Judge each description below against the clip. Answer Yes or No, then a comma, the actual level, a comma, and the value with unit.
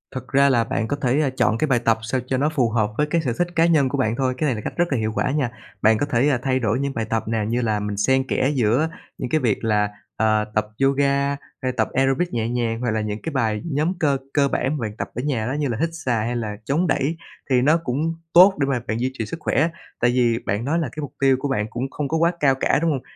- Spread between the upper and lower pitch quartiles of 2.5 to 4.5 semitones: Yes, average, 4.1 semitones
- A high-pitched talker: No, low, 130 Hz